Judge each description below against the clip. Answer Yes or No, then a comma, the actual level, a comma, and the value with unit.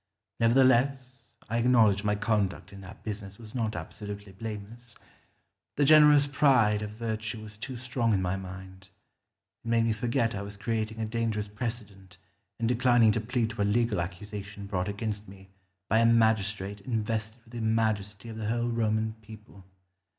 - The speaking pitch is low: Yes, low, 110 Hz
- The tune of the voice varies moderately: No, narrow, 2.3 semitones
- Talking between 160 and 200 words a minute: Yes, average, 165 wpm